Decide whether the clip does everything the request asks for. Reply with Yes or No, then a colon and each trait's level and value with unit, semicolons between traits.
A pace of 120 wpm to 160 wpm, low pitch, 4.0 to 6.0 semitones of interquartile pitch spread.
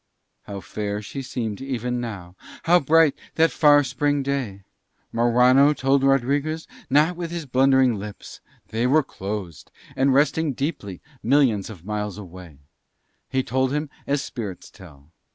Yes: average, 140 wpm; low, 130 Hz; wide, 5.4 semitones